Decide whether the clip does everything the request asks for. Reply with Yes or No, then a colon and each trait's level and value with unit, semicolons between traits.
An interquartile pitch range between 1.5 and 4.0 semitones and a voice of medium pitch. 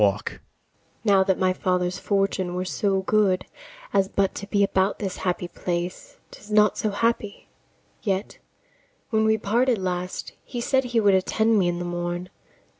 No: average, 2.7 semitones; high, 195 Hz